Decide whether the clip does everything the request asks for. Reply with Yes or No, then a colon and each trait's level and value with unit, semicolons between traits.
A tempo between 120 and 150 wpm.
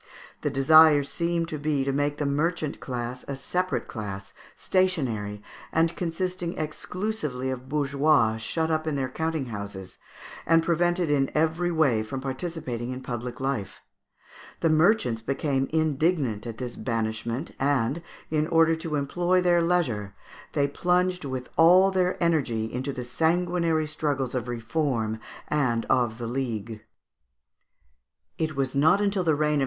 Yes: average, 140 wpm